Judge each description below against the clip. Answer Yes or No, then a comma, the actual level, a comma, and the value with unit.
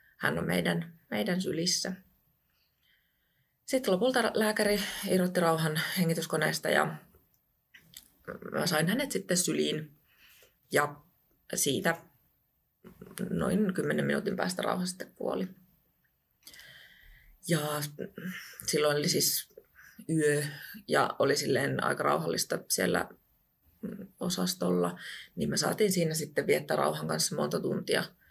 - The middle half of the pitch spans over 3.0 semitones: Yes, average, 4.3 semitones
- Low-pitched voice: No, medium, 180 Hz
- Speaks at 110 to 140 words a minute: No, average, 100 wpm